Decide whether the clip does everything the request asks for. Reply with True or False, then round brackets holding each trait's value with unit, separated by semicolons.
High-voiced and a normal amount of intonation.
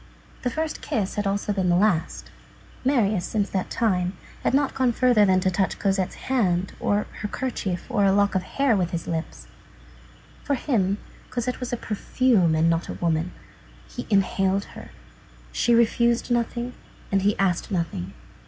True (200 Hz; 4.5 semitones)